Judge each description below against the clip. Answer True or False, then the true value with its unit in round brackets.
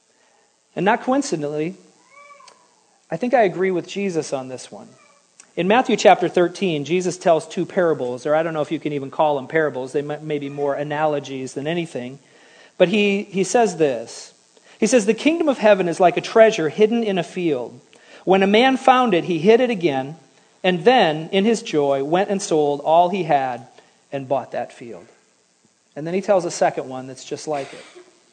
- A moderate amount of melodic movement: False (6.0 semitones)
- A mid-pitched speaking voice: True (175 Hz)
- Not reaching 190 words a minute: False (195 wpm)